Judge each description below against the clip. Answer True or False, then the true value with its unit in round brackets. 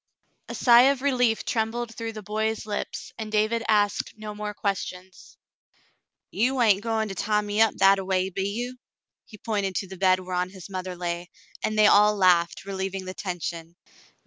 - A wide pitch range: False (2.8 semitones)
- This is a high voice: True (205 Hz)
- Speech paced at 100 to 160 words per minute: False (180 wpm)